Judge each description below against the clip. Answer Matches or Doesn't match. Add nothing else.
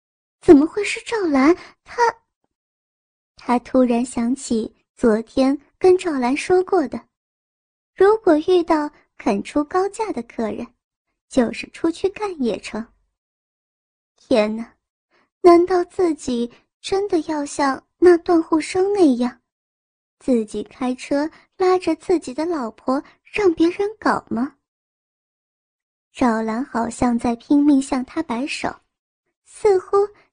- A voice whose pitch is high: Matches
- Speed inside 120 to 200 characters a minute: Matches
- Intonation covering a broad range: Matches